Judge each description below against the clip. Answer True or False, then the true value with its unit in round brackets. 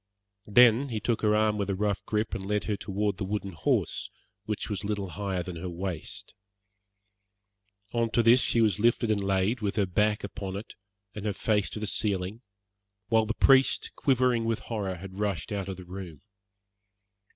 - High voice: False (105 Hz)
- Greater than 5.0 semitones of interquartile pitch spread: False (2.4 semitones)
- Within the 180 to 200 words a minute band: True (185 wpm)